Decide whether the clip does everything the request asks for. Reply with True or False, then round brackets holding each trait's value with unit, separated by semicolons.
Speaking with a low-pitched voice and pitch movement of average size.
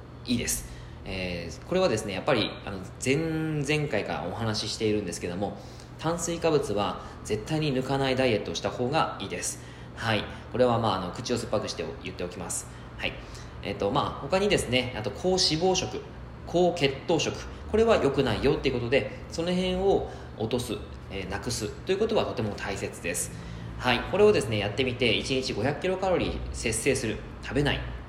False (125 Hz; 7.1 semitones)